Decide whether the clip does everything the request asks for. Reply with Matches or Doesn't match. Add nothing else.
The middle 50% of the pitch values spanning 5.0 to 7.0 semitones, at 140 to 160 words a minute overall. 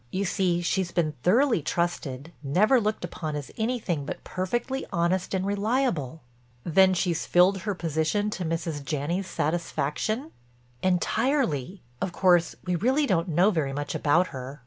Doesn't match